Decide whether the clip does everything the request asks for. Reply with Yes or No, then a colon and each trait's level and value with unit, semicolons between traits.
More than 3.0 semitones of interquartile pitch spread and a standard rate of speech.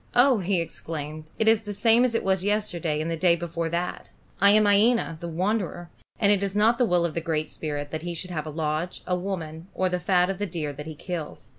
No: average, 4.1 semitones; fast, 250 wpm